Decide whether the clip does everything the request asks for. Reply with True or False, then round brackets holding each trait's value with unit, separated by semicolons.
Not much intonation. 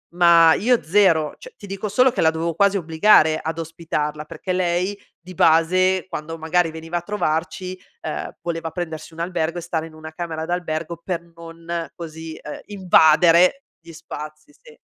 True (2.3 semitones)